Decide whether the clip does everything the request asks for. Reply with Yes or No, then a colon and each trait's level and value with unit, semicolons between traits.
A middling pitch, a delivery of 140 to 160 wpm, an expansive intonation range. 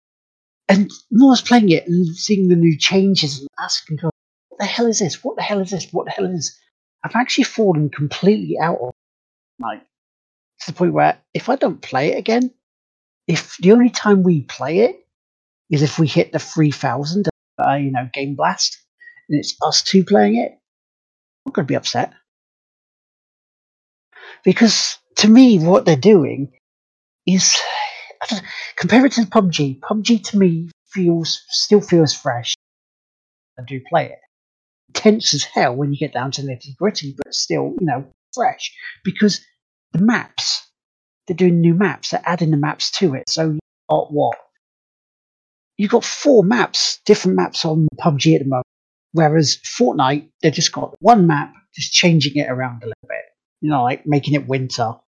No: medium, 165 Hz; average, 175 wpm; wide, 6.2 semitones